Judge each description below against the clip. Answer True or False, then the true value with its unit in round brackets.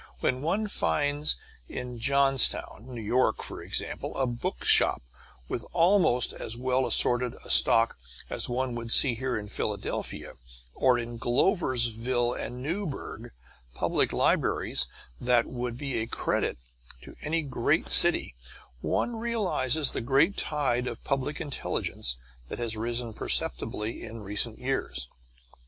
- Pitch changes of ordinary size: True (3.1 semitones)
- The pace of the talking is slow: True (130 wpm)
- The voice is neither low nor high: False (125 Hz)